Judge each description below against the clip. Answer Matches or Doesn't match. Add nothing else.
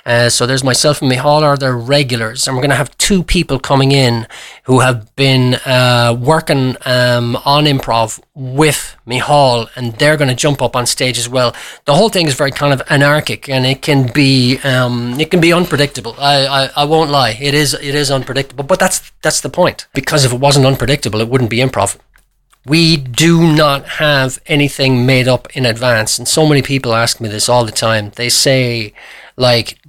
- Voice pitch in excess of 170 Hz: Doesn't match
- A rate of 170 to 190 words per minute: Doesn't match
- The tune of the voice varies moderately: Matches